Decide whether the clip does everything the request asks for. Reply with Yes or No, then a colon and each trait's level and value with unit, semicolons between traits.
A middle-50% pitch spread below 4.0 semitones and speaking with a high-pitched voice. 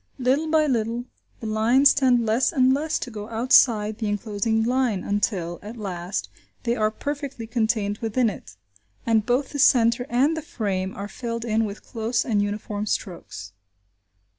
Yes: average, 3.3 semitones; high, 225 Hz